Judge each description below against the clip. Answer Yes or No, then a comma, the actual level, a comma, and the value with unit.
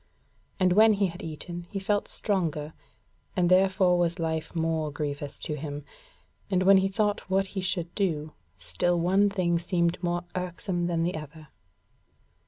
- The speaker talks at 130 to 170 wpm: Yes, average, 160 wpm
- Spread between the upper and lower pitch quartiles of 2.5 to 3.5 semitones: Yes, average, 3.0 semitones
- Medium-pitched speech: Yes, medium, 175 Hz